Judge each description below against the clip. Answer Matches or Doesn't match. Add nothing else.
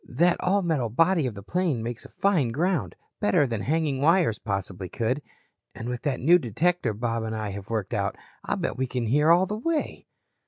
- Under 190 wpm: Doesn't match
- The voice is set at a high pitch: Doesn't match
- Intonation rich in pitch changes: Matches